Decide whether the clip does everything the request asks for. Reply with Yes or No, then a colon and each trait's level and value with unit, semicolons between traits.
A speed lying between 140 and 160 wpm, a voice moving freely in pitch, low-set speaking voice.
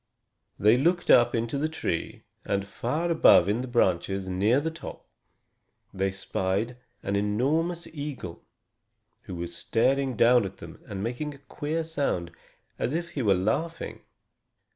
Yes: average, 145 wpm; wide, 7.2 semitones; low, 120 Hz